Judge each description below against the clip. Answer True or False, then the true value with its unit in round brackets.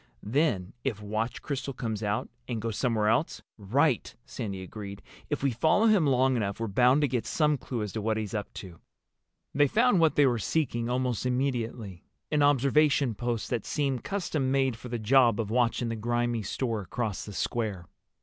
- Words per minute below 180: False (185 wpm)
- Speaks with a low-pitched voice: True (120 Hz)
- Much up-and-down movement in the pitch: False (4.1 semitones)